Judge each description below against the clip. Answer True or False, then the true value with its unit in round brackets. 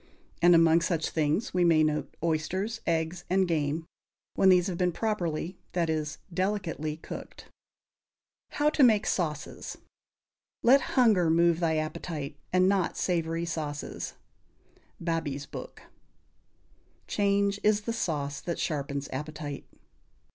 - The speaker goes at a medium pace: False (125 wpm)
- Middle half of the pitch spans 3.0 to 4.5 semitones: True (3.4 semitones)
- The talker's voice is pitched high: False (170 Hz)